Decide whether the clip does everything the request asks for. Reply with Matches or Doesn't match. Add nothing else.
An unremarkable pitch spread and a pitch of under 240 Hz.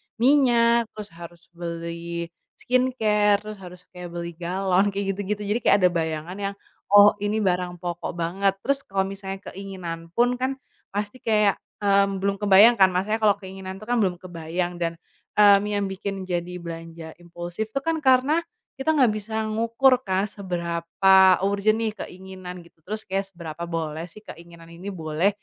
Matches